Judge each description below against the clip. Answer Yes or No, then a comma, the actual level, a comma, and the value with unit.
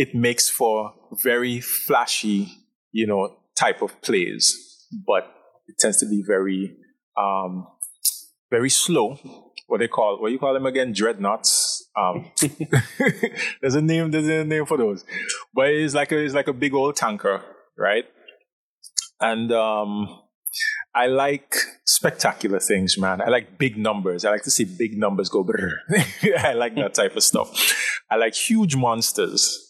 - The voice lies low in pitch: Yes, low, 130 Hz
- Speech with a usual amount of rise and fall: No, wide, 6.3 semitones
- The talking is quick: No, average, 155 wpm